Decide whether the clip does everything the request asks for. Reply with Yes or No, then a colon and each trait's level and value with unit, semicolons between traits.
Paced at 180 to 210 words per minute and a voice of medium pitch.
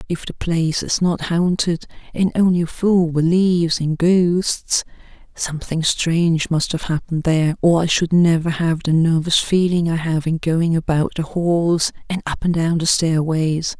No: average, 165 wpm; medium, 165 Hz